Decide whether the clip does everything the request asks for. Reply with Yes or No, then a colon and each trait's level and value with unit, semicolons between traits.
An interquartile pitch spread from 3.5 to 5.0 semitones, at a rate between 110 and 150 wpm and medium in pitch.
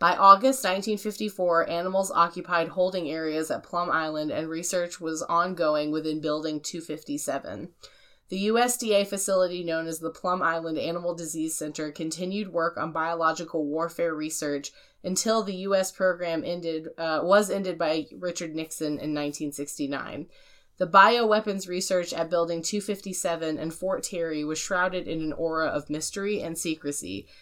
No: average, 2.9 semitones; average, 140 wpm; medium, 170 Hz